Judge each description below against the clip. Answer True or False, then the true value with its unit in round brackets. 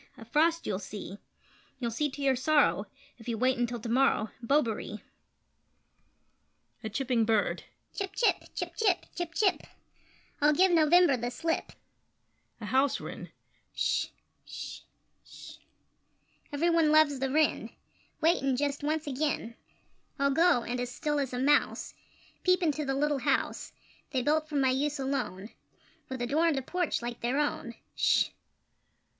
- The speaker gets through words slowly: False (155 wpm)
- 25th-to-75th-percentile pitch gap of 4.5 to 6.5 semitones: False (4.1 semitones)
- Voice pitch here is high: True (275 Hz)